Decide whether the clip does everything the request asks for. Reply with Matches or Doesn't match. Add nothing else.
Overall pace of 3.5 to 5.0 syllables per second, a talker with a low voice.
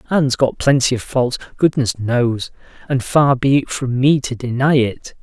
Matches